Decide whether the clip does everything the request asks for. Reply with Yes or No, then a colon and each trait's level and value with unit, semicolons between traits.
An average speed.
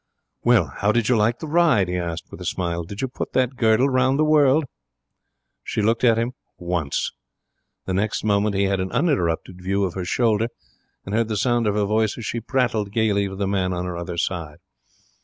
No: fast, 215 wpm